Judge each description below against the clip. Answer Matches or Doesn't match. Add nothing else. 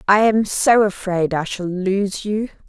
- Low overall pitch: Doesn't match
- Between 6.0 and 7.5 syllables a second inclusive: Doesn't match